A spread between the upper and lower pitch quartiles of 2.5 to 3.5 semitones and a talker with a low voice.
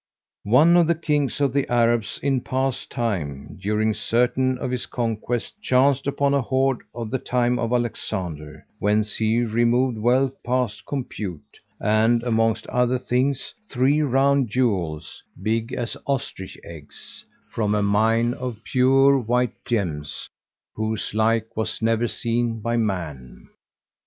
Yes: average, 3.1 semitones; low, 120 Hz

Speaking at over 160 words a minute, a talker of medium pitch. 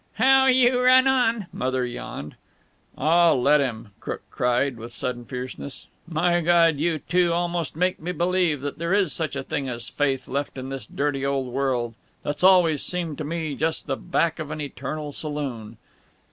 Yes: average, 175 wpm; medium, 150 Hz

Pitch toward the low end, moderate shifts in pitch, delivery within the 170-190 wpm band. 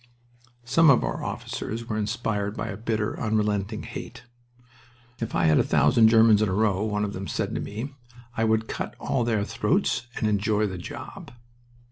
No: low, 110 Hz; narrow, 1.8 semitones; average, 180 wpm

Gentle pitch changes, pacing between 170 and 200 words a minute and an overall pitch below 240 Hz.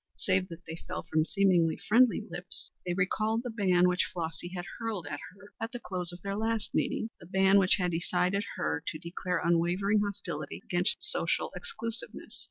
No: average, 3.1 semitones; average, 180 wpm; medium, 185 Hz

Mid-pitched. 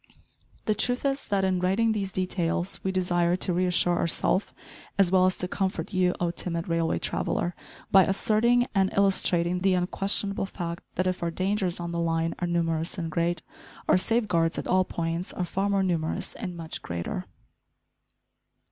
Yes: medium, 180 Hz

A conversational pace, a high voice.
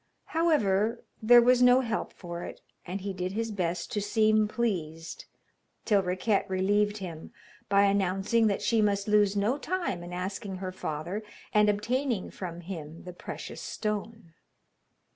Yes: average, 150 wpm; high, 200 Hz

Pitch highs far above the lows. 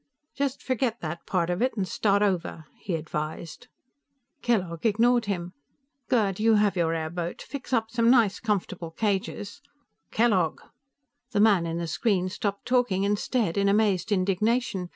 No: average, 4.3 semitones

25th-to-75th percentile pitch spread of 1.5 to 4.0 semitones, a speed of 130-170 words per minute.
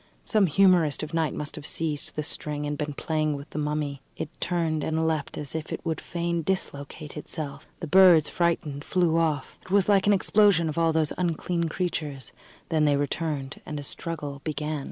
No: narrow, 2.4 semitones; average, 195 wpm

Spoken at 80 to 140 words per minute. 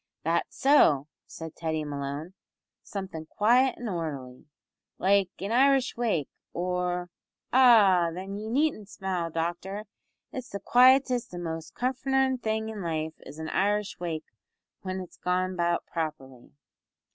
Yes: slow, 135 wpm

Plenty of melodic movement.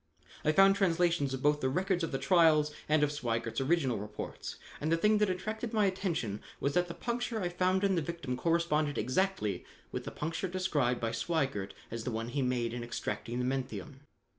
Yes: wide, 6.3 semitones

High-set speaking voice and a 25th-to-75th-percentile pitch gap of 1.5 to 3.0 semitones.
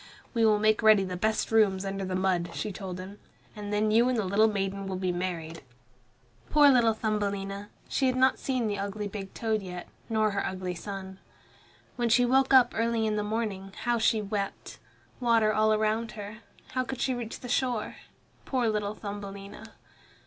Yes: high, 215 Hz; narrow, 2.6 semitones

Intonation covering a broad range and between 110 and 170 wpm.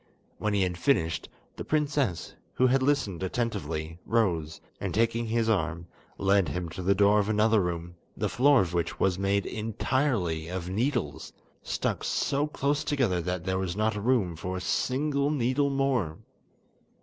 Yes: wide, 6.4 semitones; average, 160 wpm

